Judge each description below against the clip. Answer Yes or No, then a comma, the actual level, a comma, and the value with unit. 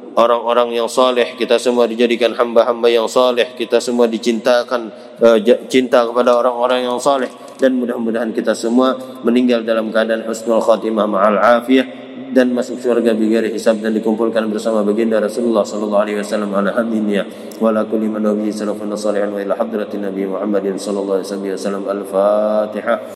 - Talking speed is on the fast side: No, average, 125 wpm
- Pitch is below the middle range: Yes, low, 115 Hz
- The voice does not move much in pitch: Yes, narrow, 2.3 semitones